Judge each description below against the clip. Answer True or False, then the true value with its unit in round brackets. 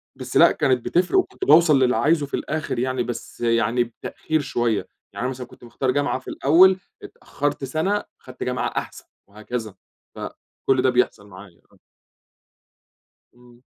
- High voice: False (130 Hz)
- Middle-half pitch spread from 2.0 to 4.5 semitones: True (3.5 semitones)